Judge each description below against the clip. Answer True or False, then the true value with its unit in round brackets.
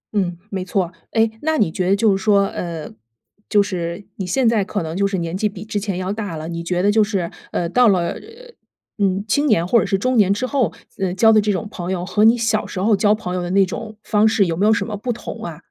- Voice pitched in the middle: False (200 Hz)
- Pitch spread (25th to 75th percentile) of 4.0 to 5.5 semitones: False (3.2 semitones)